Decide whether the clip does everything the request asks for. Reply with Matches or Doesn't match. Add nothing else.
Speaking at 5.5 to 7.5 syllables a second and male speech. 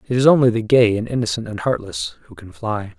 Matches